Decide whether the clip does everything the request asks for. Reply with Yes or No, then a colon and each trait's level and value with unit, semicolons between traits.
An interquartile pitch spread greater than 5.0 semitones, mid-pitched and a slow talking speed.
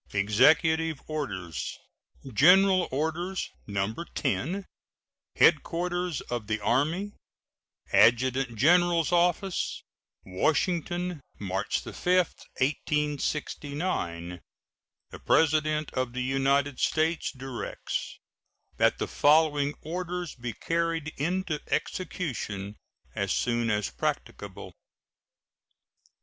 Yes: wide, 5.6 semitones; medium, 150 Hz; slow, 85 wpm